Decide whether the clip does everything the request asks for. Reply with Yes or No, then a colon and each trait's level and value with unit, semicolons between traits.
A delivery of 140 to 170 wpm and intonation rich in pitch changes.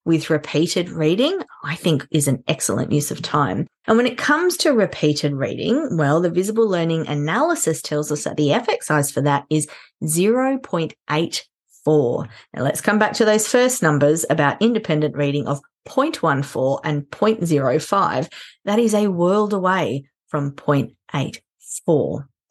Yes: average, 145 wpm; wide, 6.4 semitones